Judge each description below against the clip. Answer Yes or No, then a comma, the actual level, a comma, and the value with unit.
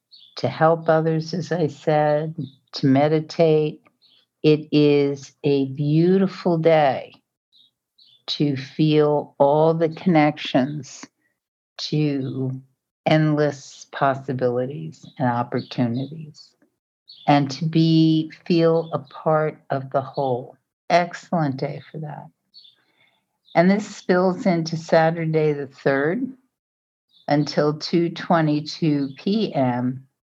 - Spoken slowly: Yes, slow, 90 wpm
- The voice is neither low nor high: Yes, medium, 150 Hz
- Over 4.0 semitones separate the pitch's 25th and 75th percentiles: No, narrow, 2.6 semitones